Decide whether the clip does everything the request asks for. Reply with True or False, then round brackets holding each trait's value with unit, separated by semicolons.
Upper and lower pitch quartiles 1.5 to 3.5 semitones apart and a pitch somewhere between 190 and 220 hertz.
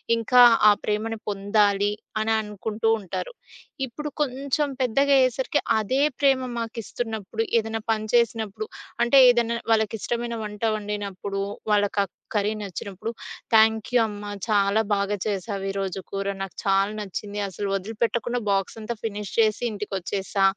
True (2.4 semitones; 215 Hz)